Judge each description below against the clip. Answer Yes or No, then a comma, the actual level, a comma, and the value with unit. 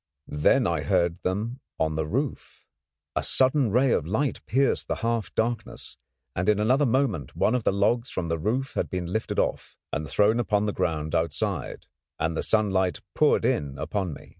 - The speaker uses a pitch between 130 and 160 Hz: No, low, 105 Hz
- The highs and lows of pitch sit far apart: Yes, wide, 6.3 semitones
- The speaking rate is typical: Yes, average, 185 wpm